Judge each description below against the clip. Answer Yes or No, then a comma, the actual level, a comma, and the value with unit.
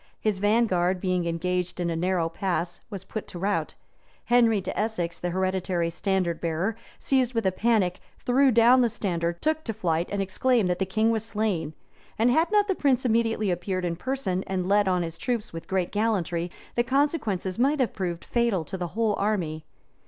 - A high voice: Yes, high, 195 Hz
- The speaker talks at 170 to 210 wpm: Yes, average, 190 wpm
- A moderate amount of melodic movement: Yes, average, 4.5 semitones